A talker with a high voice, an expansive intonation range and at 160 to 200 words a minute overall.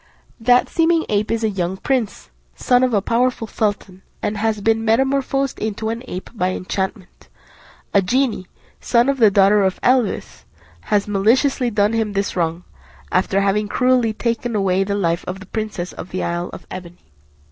No: high, 210 Hz; average, 3.8 semitones; average, 170 wpm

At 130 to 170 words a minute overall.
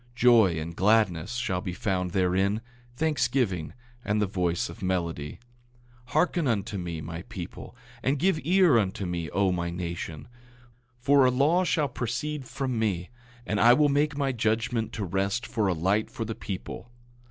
Yes: average, 165 wpm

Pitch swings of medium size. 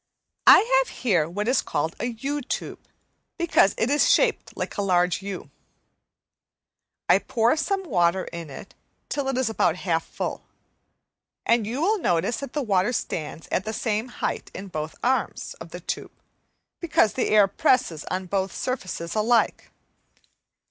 No: wide, 6.1 semitones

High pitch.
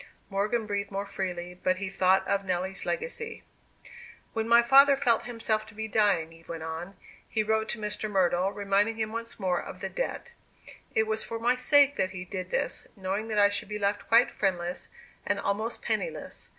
Yes: high, 205 Hz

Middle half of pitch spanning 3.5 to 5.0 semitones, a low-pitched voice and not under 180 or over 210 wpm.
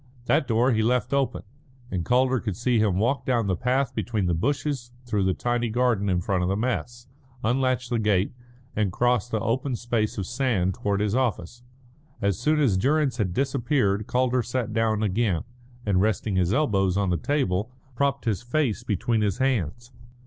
Yes: average, 4.0 semitones; low, 115 Hz; average, 185 wpm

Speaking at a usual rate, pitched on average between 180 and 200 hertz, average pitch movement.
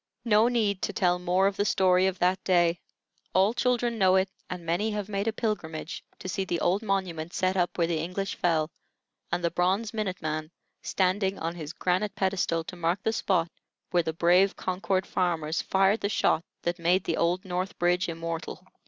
No: average, 195 wpm; medium, 185 Hz; narrow, 2.3 semitones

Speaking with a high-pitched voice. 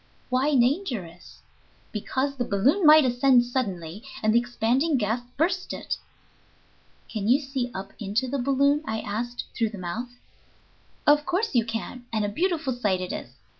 Yes: high, 245 Hz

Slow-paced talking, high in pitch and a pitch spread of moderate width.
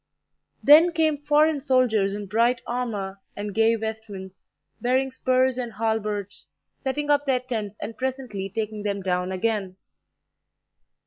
Yes: slow, 130 wpm; high, 225 Hz; average, 4.3 semitones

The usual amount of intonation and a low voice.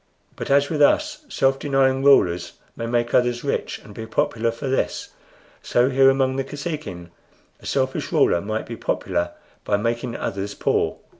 Yes: average, 3.6 semitones; low, 125 Hz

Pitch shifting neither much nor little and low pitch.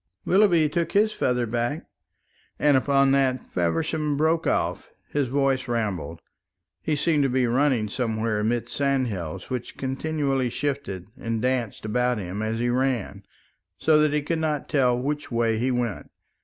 Yes: average, 4.1 semitones; low, 130 Hz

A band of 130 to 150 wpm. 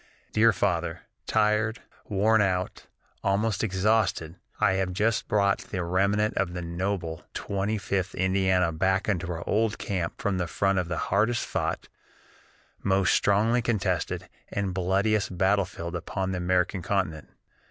Yes: average, 140 wpm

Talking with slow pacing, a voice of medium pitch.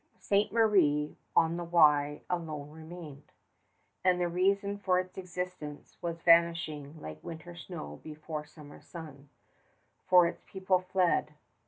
Yes: slow, 130 wpm; medium, 170 Hz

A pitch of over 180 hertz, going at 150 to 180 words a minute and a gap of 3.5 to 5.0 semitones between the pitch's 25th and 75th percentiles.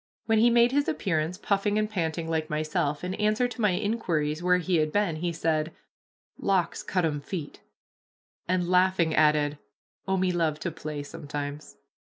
No: medium, 170 Hz; average, 170 wpm; average, 4.1 semitones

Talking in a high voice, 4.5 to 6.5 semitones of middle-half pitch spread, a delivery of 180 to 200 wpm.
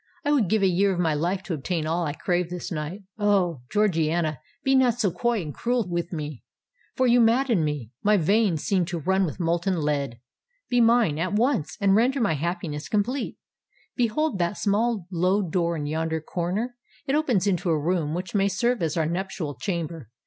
No: medium, 180 Hz; average, 4.8 semitones; average, 185 wpm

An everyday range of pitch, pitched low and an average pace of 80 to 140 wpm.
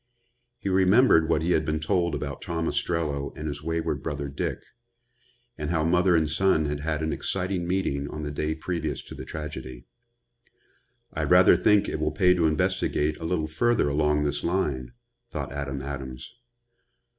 No: average, 3.0 semitones; very low, 80 Hz; average, 170 wpm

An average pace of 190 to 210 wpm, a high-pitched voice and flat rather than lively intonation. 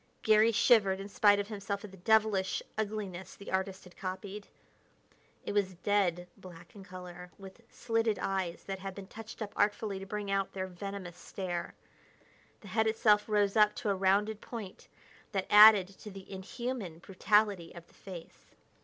No: average, 170 wpm; high, 200 Hz; narrow, 2.0 semitones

